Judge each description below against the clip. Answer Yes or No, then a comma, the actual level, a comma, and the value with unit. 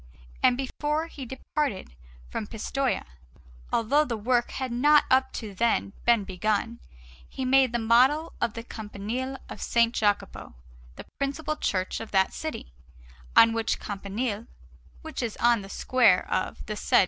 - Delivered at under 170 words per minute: Yes, average, 155 wpm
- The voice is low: No, high, 235 Hz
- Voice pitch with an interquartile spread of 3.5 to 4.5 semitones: Yes, average, 3.9 semitones